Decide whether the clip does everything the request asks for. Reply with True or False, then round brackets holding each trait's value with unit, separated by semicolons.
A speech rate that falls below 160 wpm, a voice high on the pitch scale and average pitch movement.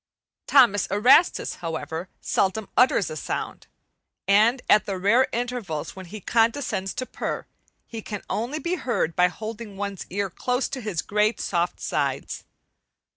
True (145 wpm; 210 Hz; 4.2 semitones)